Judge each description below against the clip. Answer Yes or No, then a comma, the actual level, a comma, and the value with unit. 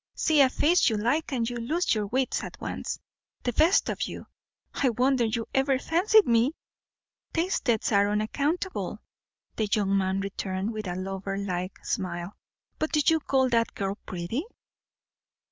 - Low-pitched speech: No, high, 230 Hz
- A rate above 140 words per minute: Yes, average, 160 wpm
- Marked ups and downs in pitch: Yes, wide, 6.1 semitones